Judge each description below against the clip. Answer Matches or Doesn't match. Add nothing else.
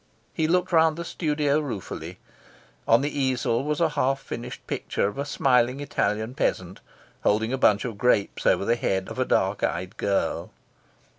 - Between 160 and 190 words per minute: Matches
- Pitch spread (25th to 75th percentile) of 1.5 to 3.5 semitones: Doesn't match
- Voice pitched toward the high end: Doesn't match